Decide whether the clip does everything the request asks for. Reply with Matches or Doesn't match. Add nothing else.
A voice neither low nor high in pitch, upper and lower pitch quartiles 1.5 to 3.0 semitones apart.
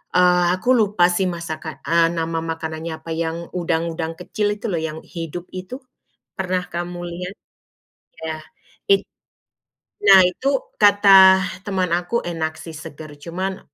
Matches